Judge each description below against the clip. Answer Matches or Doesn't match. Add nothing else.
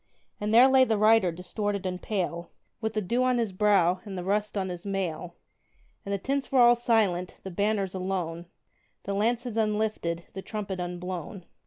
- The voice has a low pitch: Doesn't match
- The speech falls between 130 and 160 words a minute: Doesn't match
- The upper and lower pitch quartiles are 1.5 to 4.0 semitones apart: Matches